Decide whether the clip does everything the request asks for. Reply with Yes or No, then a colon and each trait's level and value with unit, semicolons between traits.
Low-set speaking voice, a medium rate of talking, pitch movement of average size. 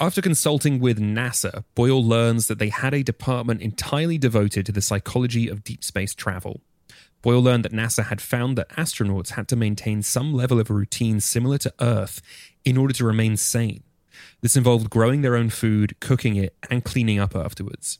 Yes: low, 115 Hz; average, 185 wpm; average, 3.2 semitones